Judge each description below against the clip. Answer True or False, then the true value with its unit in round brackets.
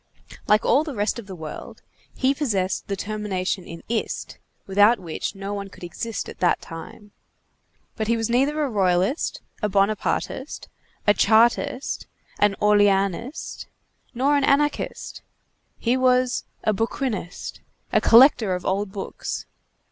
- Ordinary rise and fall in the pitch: True (4.4 semitones)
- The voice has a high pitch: True (210 Hz)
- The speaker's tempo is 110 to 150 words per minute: True (140 wpm)